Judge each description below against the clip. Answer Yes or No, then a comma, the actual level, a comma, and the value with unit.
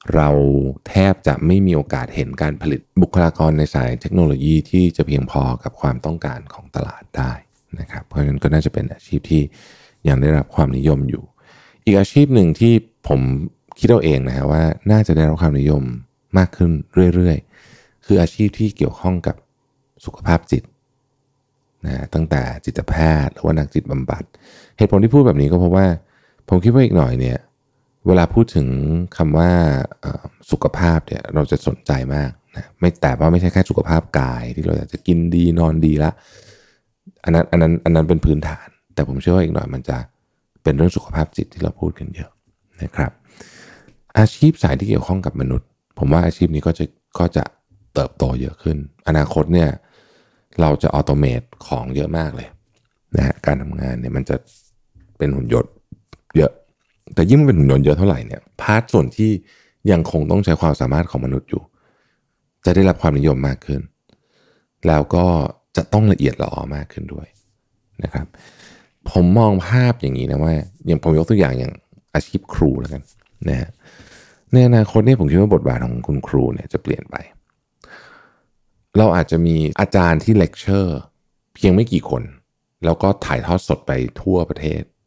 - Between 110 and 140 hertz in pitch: No, very low, 85 Hz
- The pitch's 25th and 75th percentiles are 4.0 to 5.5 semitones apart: Yes, average, 5.1 semitones